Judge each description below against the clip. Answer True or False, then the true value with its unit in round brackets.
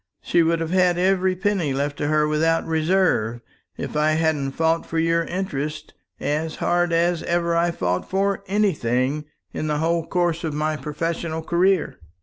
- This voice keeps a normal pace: True (165 wpm)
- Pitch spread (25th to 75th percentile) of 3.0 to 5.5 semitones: False (2.4 semitones)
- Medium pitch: True (165 Hz)